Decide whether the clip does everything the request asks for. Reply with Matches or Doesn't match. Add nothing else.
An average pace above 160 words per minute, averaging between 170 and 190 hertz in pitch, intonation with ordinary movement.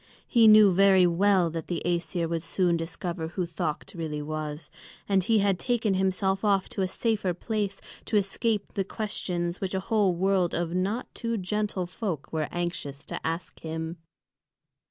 Matches